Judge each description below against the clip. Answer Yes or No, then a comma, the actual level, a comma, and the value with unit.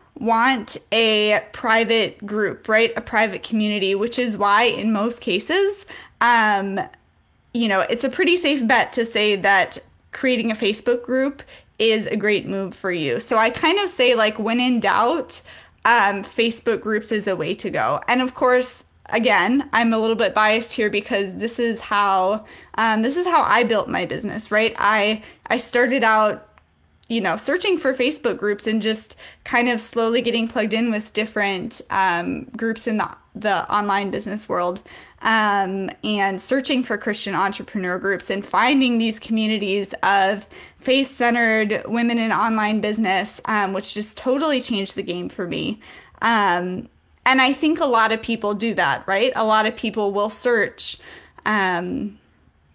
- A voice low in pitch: No, high, 220 Hz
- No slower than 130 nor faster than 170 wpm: Yes, average, 165 wpm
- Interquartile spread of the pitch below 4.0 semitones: Yes, average, 2.7 semitones